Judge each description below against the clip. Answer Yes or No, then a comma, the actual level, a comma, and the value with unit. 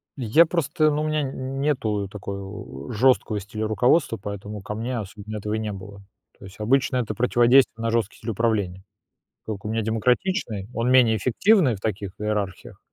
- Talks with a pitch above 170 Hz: No, low, 110 Hz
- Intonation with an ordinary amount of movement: Yes, average, 3.9 semitones